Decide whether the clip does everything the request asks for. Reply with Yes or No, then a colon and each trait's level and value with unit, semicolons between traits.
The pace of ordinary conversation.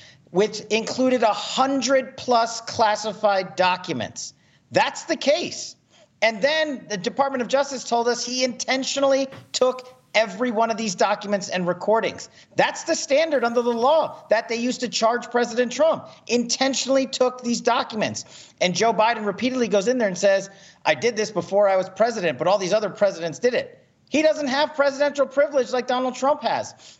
Yes: average, 170 wpm